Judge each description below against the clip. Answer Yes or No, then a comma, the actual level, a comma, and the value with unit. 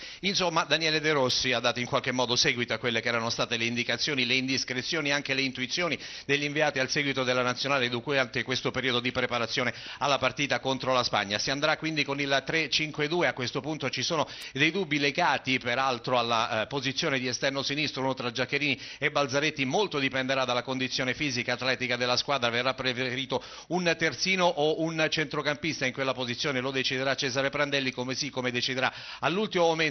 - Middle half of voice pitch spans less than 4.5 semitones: Yes, average, 2.9 semitones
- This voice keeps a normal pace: No, fast, 185 wpm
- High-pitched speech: No, low, 135 Hz